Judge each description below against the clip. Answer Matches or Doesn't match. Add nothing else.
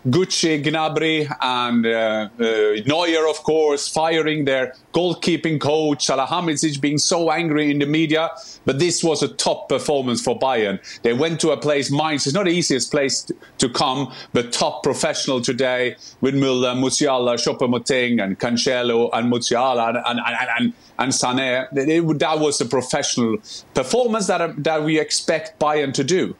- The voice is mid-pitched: Matches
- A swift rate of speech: Doesn't match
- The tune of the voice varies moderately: Matches